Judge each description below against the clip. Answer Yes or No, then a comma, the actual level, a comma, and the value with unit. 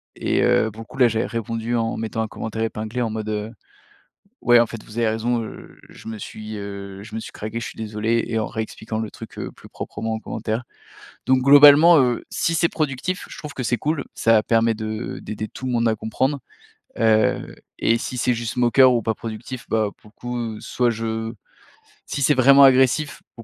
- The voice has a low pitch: Yes, low, 115 Hz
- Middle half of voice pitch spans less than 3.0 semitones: Yes, narrow, 2.4 semitones